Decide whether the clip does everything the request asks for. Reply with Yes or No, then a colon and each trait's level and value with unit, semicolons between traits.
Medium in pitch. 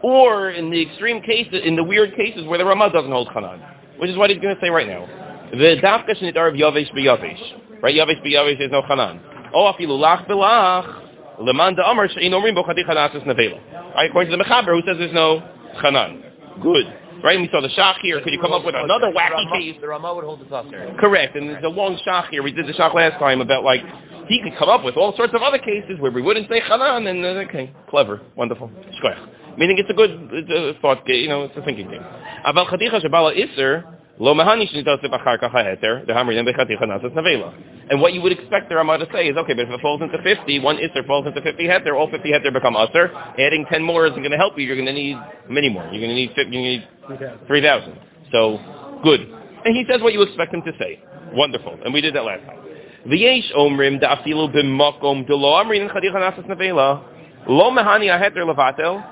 Yes: medium, 165 Hz